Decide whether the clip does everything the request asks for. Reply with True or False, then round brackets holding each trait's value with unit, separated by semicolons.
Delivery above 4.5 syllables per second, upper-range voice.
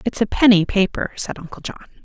True (5.8 syllables/s; 205 Hz)